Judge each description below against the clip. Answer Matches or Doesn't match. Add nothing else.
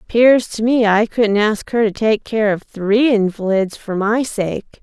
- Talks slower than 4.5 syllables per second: Matches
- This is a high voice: Matches